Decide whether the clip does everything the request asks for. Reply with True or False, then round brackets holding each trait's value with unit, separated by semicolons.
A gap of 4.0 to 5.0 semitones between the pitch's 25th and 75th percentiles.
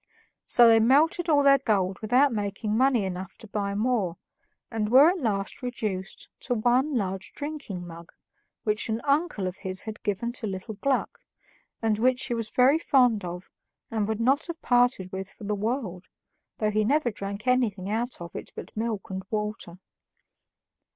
True (4.3 semitones)